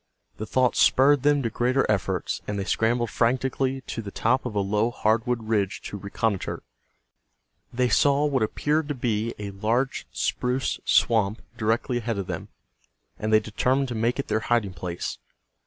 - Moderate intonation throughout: Yes, average, 3.4 semitones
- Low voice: Yes, low, 115 Hz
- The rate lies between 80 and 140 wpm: No, average, 170 wpm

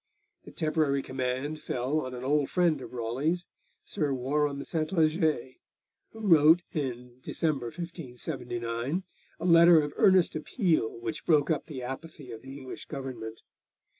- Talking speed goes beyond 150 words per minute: No, slow, 135 wpm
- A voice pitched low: No, medium, 145 Hz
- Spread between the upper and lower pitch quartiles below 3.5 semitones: No, average, 4.2 semitones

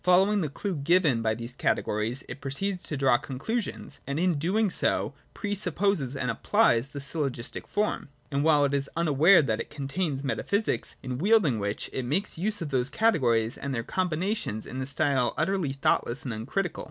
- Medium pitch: Yes, medium, 145 Hz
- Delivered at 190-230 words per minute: Yes, average, 195 wpm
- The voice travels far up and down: Yes, wide, 6.3 semitones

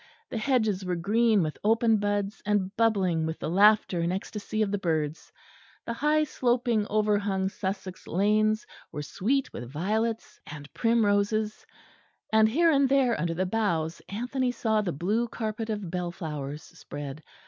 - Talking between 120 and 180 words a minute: Yes, average, 155 wpm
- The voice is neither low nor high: No, high, 205 Hz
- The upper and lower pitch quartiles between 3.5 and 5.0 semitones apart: Yes, average, 4.2 semitones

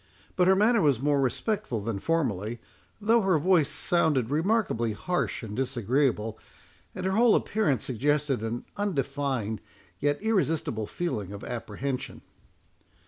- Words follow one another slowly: Yes, slow, 130 wpm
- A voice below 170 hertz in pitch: Yes, medium, 140 Hz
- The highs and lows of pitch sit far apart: Yes, wide, 7.9 semitones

